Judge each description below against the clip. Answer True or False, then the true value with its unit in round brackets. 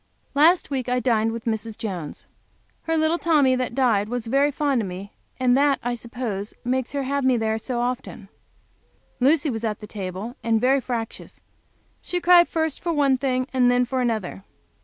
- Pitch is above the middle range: True (250 Hz)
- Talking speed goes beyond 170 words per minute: True (180 wpm)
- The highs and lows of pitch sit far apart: False (3.7 semitones)